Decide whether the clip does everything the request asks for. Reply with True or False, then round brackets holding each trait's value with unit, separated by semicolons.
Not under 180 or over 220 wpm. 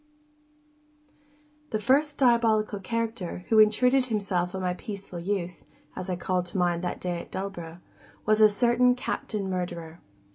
False (145 wpm)